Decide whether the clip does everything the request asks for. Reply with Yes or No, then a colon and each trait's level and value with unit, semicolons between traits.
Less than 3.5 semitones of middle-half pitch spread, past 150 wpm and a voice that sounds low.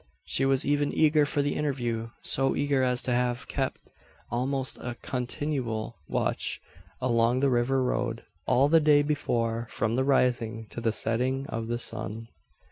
Yes: average, 3.1 semitones; average, 160 wpm; low, 125 Hz